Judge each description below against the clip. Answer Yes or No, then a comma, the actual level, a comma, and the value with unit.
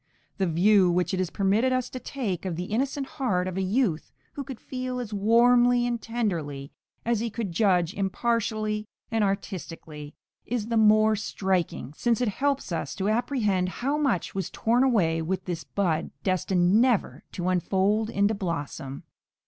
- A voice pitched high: Yes, high, 205 Hz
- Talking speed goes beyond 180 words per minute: No, average, 165 wpm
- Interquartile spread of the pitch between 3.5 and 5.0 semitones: Yes, average, 4.7 semitones